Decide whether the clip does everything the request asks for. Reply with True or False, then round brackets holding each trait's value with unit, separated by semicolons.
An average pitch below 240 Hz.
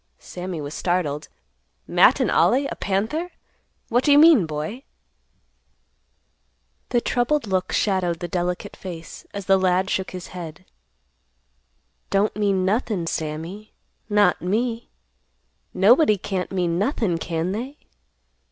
True (190 Hz)